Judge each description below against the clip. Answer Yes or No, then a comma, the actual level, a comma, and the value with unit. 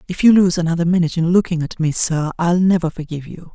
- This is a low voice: No, medium, 170 Hz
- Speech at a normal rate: No, fast, 235 wpm